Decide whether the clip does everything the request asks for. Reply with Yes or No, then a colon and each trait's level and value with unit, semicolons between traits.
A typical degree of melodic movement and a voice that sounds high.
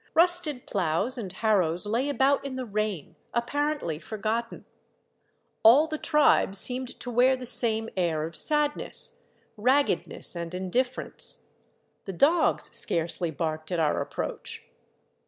No: wide, 7.1 semitones; high, 230 Hz